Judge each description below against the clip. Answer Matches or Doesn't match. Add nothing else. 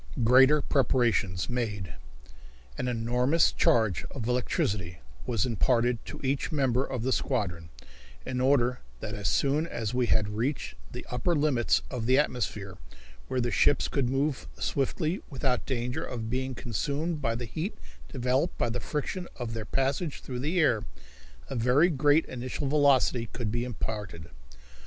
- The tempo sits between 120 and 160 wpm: Matches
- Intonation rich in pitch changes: Doesn't match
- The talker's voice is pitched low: Matches